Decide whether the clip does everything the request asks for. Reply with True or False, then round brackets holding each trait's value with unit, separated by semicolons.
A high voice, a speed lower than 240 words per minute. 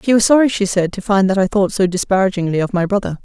False (195 Hz; 280 wpm)